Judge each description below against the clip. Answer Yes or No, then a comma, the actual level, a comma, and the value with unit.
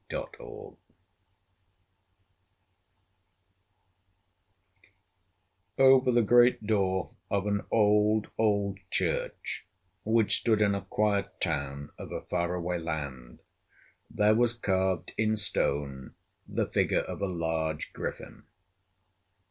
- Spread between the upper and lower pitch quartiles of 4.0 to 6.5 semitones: Yes, average, 4.3 semitones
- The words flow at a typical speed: No, slow, 95 wpm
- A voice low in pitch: Yes, low, 100 Hz